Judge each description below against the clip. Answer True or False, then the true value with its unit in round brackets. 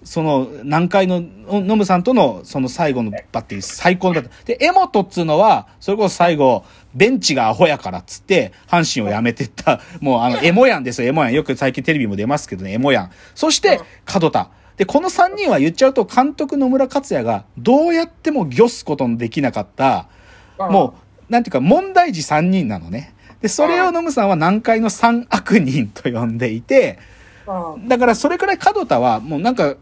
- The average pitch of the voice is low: False (195 Hz)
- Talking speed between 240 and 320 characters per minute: False (370 characters per minute)